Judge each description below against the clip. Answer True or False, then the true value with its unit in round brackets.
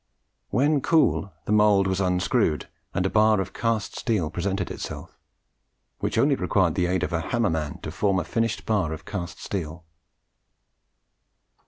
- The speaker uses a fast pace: False (155 wpm)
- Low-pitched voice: True (95 Hz)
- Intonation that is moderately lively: True (3.9 semitones)